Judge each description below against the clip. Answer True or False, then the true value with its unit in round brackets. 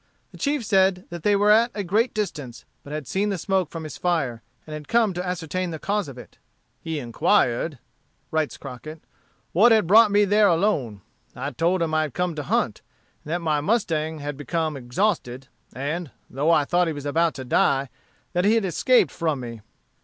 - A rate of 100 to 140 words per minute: False (200 wpm)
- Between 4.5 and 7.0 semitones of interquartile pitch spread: True (5.1 semitones)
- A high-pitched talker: False (165 Hz)